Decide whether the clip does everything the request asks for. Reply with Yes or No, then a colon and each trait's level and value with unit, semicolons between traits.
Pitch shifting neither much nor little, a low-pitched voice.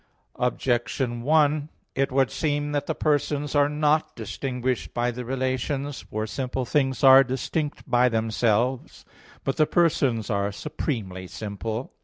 Yes: average, 3.5 semitones; low, 130 Hz